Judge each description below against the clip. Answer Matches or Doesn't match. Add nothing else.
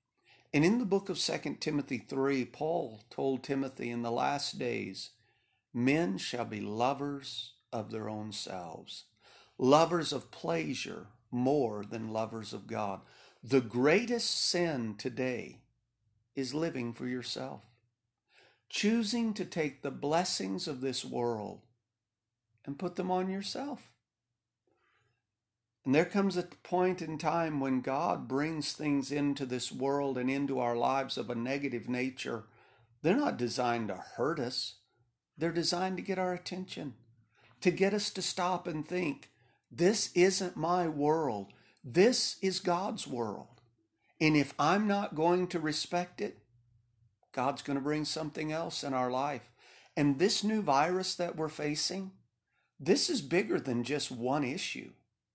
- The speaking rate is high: Doesn't match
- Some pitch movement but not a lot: Doesn't match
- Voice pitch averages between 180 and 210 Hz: Doesn't match